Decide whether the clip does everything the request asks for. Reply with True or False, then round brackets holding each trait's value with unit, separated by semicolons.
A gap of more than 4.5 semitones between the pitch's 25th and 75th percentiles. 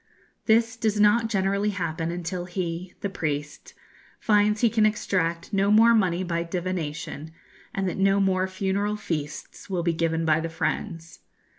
False (3.7 semitones)